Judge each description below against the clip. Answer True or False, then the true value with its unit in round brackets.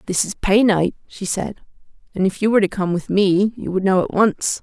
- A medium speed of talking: False (245 wpm)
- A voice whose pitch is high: True (195 Hz)